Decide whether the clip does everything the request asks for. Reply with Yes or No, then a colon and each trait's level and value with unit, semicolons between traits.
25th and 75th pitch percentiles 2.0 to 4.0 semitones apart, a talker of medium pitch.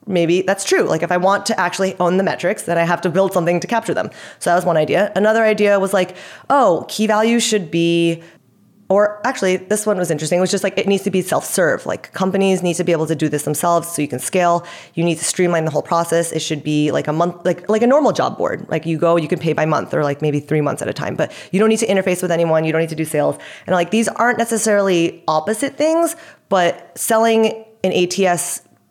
Yes: average, 3.6 semitones; medium, 180 Hz